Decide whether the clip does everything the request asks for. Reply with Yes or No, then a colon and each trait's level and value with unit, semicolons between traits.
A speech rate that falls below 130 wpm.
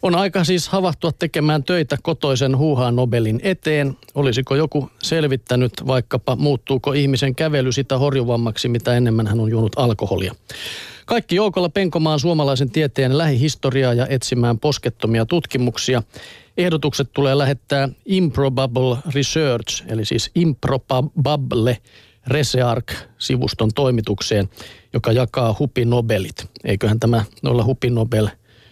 Yes: average, 115 wpm